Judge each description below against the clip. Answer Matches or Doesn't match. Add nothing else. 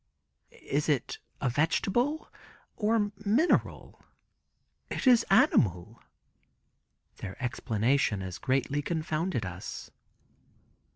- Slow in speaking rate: Matches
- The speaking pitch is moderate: Matches